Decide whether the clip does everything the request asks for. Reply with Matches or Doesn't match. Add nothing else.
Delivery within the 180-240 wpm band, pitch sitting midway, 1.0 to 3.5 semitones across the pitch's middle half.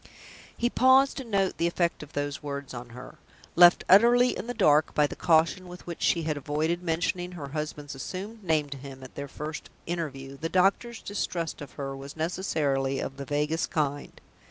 Doesn't match